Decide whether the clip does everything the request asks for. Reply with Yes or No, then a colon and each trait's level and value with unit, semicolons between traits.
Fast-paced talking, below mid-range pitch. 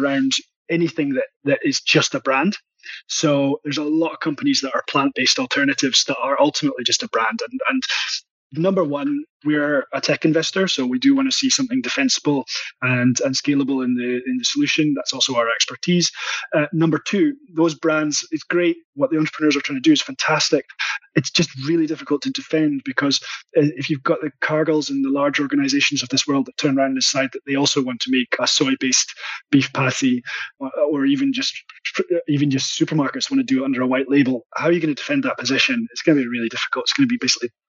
No: fast, 220 wpm; medium, 160 Hz